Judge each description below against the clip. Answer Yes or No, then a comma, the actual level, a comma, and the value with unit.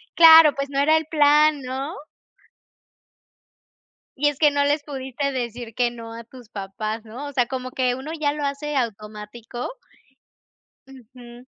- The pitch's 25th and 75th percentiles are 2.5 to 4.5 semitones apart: Yes, average, 3.4 semitones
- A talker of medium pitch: No, very high, 260 Hz